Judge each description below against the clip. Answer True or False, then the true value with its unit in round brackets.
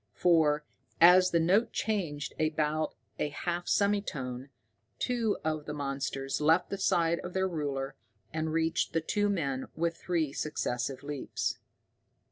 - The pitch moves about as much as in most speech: True (3.5 semitones)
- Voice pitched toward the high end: False (160 Hz)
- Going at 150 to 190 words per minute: False (135 wpm)